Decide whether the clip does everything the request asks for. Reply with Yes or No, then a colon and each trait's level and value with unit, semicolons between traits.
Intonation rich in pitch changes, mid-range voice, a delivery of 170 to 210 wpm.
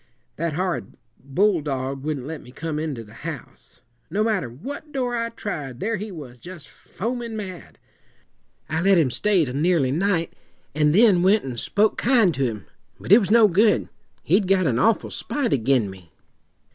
Yes: wide, 7.5 semitones; medium, 170 Hz; average, 175 wpm